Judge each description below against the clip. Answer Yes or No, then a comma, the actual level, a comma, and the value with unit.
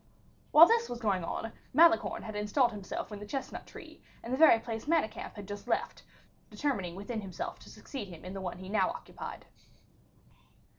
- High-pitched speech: Yes, high, 215 Hz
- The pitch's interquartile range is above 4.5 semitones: Yes, average, 5.3 semitones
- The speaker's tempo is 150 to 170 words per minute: No, average, 185 wpm